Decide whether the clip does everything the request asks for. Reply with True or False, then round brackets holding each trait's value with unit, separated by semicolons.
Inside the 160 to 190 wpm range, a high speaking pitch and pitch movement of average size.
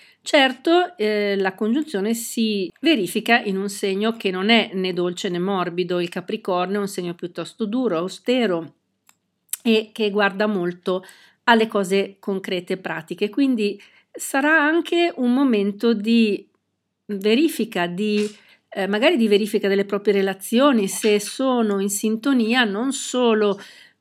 False (135 wpm; 210 Hz; 3.4 semitones)